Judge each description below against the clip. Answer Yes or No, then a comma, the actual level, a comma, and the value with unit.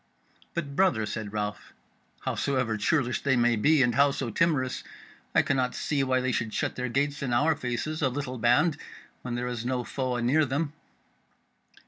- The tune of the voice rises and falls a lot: No, average, 2.9 semitones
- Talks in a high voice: No, low, 130 Hz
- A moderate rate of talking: Yes, average, 170 wpm